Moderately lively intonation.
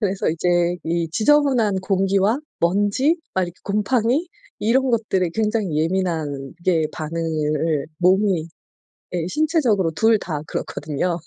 Yes: average, 4.8 semitones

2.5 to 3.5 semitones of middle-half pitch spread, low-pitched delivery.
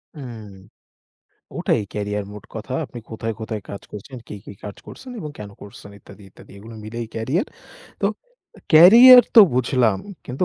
No: average, 5.2 semitones; low, 115 Hz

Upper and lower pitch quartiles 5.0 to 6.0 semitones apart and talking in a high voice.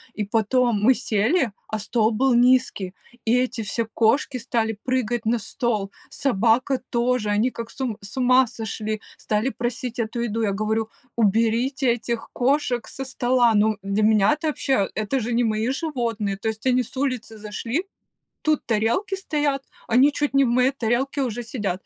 No: average, 3.0 semitones; high, 235 Hz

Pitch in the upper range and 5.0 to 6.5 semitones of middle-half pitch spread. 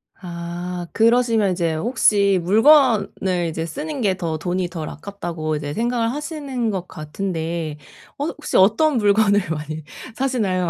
Yes: high, 195 Hz; wide, 5.5 semitones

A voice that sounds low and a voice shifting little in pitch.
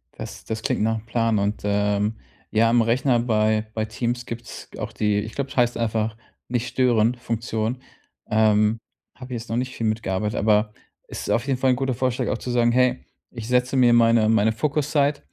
Yes: low, 115 Hz; narrow, 2.3 semitones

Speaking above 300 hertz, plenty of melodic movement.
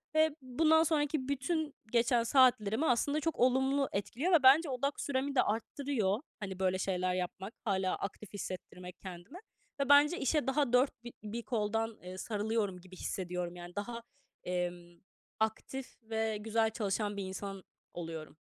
No: high, 225 Hz; wide, 6.2 semitones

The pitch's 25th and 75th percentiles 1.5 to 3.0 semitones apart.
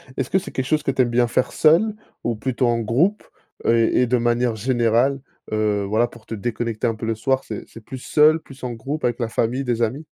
Yes: average, 2.7 semitones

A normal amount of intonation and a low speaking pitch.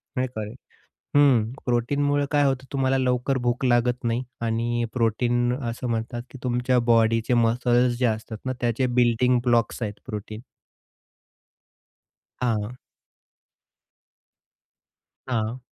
No: narrow, 1.7 semitones; low, 120 Hz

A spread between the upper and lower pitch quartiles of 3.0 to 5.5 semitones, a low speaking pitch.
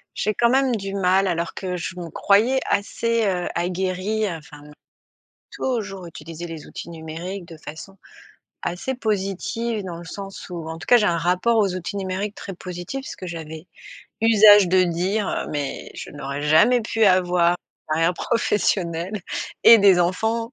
No: average, 3.7 semitones; medium, 185 Hz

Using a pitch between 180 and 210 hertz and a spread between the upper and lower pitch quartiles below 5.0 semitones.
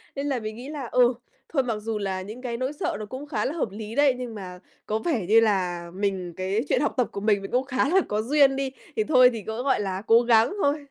No: high, 230 Hz; average, 4.5 semitones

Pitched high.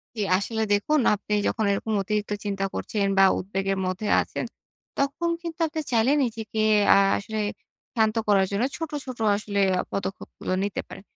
Yes: high, 210 Hz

